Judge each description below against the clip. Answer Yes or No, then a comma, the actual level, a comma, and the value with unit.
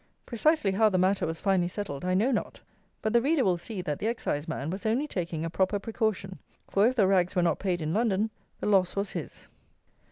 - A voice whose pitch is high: Yes, high, 195 Hz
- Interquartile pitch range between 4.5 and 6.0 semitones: No, average, 3.6 semitones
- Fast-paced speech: Yes, fast, 220 wpm